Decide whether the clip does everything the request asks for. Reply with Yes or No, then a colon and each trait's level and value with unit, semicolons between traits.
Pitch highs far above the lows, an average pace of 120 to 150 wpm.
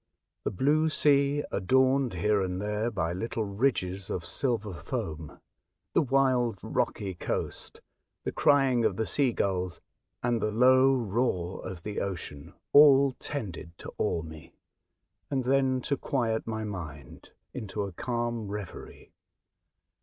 Yes: wide, 5.8 semitones; slow, 135 wpm